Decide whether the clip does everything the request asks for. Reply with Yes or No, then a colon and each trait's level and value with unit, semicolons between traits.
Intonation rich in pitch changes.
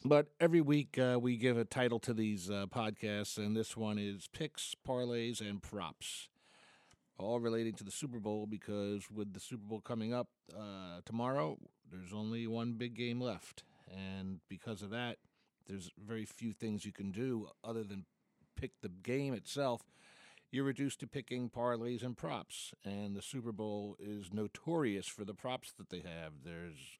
No: average, 3.3 semitones